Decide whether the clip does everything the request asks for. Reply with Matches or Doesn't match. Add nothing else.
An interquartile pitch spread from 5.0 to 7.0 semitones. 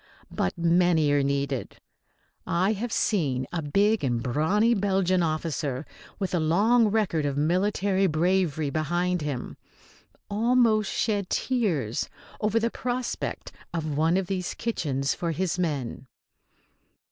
Matches